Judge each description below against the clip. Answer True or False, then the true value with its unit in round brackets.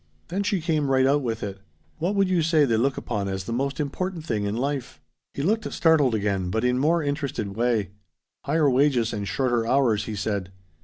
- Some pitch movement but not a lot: False (5.8 semitones)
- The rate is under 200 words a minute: False (205 wpm)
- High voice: False (130 Hz)